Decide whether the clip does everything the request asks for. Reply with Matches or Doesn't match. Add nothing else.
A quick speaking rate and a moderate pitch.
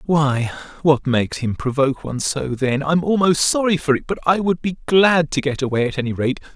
Matches